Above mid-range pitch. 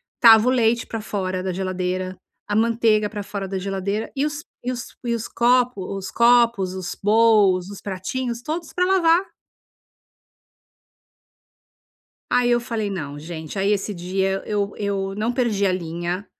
Yes: high, 205 Hz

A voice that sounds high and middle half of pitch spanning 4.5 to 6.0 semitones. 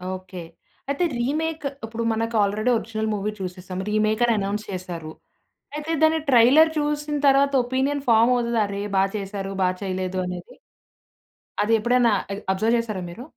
Yes: high, 225 Hz; average, 5.0 semitones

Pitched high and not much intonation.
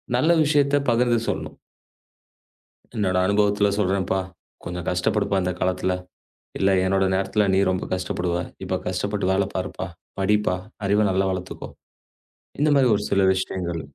No: very low, 95 Hz; narrow, 2.1 semitones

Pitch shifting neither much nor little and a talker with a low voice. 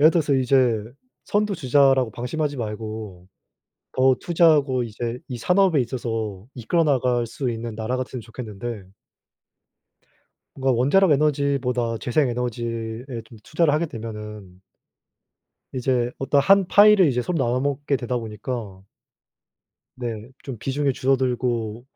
Yes: average, 3.7 semitones; low, 125 Hz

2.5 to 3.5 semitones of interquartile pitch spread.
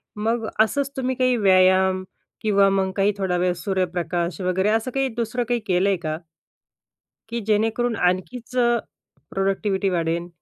No: average, 4.0 semitones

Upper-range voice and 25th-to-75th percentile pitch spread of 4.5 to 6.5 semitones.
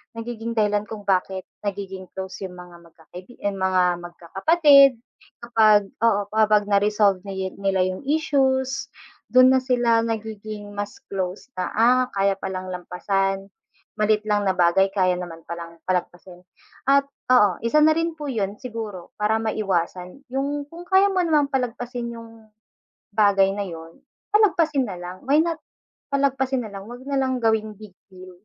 Yes: high, 210 Hz; average, 5.1 semitones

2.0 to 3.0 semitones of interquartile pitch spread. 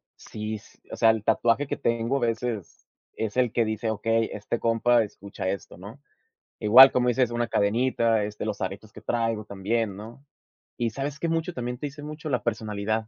Yes: narrow, 2.6 semitones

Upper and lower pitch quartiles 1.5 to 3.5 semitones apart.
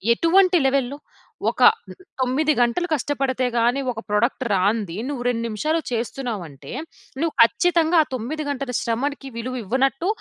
No: average, 3.9 semitones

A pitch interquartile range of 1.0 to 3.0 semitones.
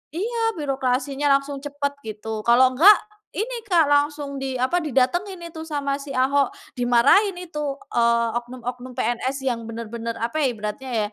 No: average, 3.8 semitones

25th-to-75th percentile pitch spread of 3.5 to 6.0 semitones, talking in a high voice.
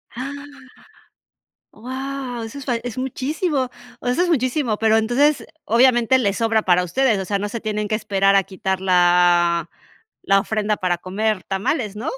Yes: average, 4.8 semitones; high, 220 Hz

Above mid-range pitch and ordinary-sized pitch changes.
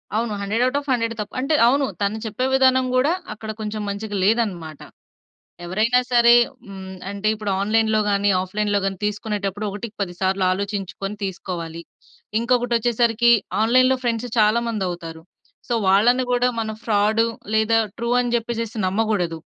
Yes: high, 215 Hz; average, 3.0 semitones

